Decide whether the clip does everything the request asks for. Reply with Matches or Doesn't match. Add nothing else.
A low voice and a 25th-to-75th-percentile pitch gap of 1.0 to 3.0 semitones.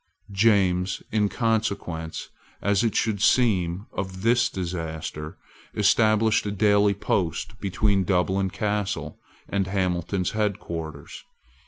Matches